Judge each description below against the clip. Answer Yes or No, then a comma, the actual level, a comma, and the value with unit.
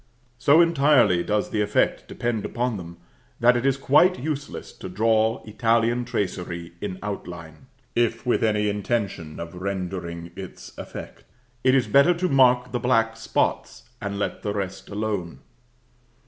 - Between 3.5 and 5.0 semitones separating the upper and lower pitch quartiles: Yes, average, 4.5 semitones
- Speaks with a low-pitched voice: Yes, low, 110 Hz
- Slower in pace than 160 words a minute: Yes, average, 150 wpm